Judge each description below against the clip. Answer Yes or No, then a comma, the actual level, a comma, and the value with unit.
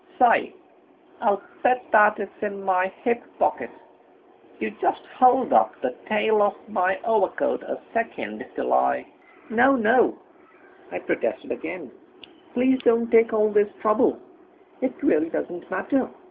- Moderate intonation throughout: Yes, average, 3.6 semitones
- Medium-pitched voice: No, high, 215 Hz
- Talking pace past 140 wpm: No, slow, 135 wpm